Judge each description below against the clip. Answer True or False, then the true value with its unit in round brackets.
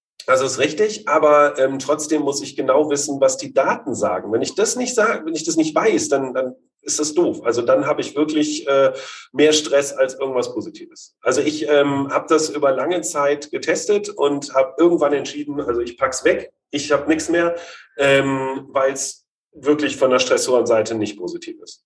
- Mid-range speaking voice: True (145 Hz)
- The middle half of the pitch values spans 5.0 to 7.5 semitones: False (3.6 semitones)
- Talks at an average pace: False (200 wpm)